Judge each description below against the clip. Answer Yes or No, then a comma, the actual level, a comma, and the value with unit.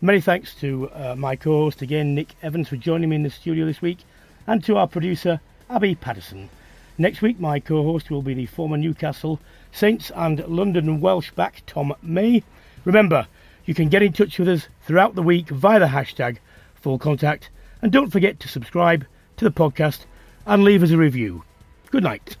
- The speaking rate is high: No, average, 190 wpm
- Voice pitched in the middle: Yes, medium, 160 Hz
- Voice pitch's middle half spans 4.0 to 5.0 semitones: Yes, average, 4.5 semitones